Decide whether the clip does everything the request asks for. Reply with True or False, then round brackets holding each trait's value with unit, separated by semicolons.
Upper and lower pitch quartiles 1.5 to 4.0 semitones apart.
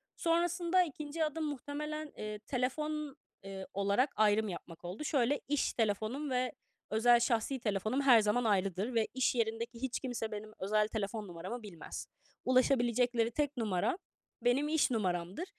False (5.0 semitones)